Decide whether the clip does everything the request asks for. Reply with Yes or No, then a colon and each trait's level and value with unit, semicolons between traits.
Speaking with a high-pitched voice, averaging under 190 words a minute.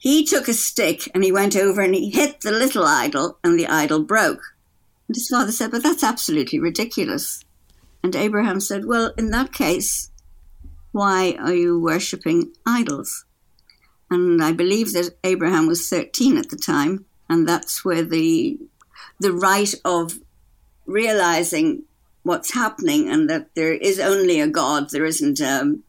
Yes: high, 210 Hz; average, 160 wpm